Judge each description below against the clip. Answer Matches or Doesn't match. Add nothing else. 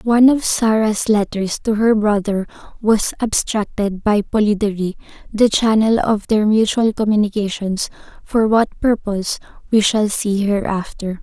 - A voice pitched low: Doesn't match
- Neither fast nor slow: Doesn't match